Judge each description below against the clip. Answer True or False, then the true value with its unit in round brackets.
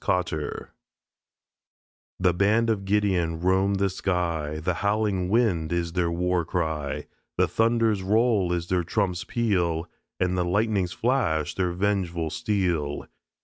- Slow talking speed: True (130 wpm)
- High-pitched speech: False (90 Hz)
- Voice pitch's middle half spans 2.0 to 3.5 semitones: True (3.2 semitones)